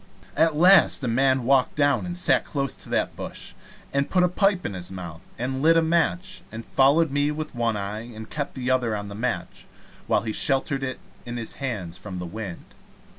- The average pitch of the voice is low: Yes, low, 130 Hz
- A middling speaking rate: No, fast, 215 wpm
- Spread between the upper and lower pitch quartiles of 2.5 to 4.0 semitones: No, wide, 5.6 semitones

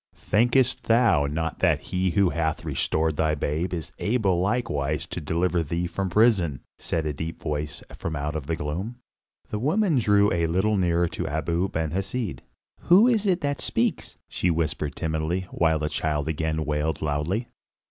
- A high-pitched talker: No, very low, 85 Hz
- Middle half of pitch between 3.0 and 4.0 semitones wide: No, average, 4.8 semitones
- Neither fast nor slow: Yes, average, 170 wpm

